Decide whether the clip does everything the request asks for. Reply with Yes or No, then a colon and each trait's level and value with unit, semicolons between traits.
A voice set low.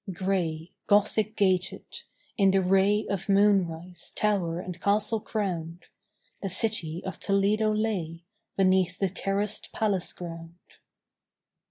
No: high, 195 Hz